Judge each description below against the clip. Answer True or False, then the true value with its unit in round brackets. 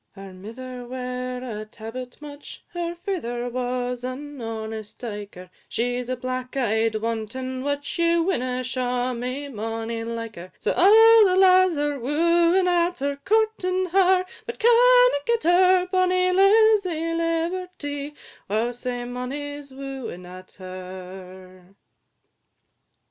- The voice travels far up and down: True (7.2 semitones)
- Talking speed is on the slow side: True (130 wpm)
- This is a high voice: True (255 Hz)